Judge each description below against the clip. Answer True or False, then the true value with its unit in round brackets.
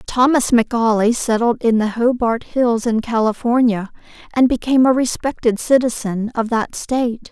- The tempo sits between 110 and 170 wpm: True (140 wpm)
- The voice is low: False (235 Hz)